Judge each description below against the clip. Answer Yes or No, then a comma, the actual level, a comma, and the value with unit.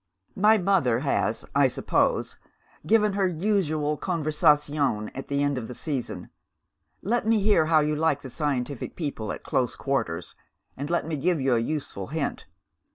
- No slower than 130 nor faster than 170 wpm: Yes, average, 160 wpm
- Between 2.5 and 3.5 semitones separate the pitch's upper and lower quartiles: No, average, 4.5 semitones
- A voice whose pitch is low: No, medium, 150 Hz